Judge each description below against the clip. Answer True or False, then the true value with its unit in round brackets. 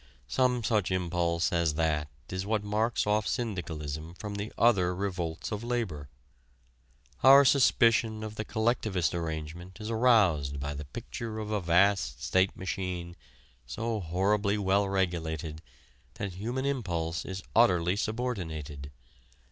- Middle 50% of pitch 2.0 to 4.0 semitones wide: False (4.6 semitones)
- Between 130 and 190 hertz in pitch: False (95 Hz)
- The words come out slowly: True (130 wpm)